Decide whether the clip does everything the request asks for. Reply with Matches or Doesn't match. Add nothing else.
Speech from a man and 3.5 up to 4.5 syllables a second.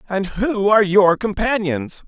Matches